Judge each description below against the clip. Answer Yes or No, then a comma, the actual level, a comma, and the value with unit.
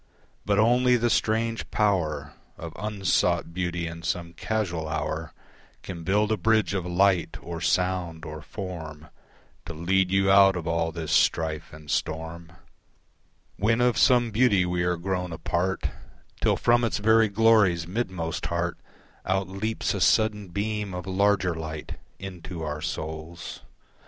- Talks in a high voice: No, very low, 90 Hz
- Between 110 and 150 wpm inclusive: Yes, average, 145 wpm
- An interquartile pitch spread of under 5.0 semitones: Yes, average, 3.9 semitones